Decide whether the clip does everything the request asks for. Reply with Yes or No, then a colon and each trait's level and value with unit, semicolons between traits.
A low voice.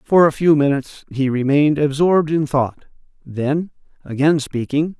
No: medium, 145 Hz